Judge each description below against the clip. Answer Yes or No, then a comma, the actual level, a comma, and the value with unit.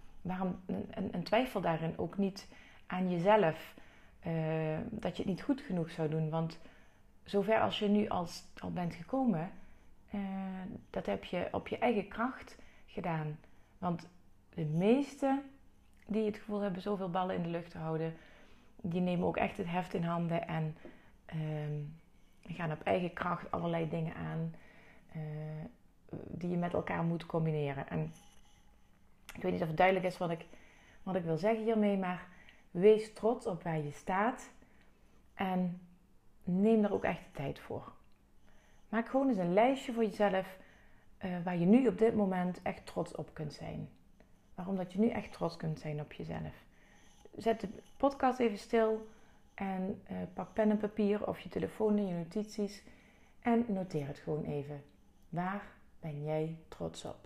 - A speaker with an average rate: Yes, average, 170 wpm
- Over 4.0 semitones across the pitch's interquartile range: Yes, average, 4.6 semitones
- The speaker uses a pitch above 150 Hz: Yes, medium, 185 Hz